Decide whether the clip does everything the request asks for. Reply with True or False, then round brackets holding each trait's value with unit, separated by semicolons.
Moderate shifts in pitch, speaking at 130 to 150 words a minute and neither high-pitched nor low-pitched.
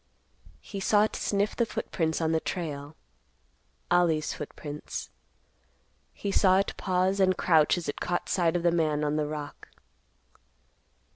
True (3.8 semitones; 140 wpm; 165 Hz)